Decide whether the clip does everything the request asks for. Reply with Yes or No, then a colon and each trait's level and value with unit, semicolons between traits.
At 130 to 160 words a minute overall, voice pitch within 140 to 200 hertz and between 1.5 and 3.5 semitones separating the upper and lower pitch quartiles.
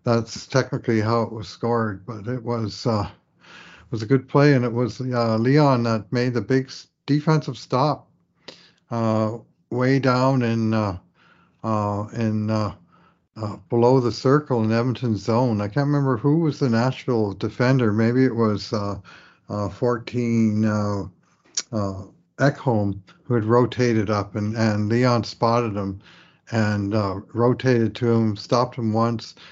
No: average, 155 wpm; low, 115 Hz; average, 2.8 semitones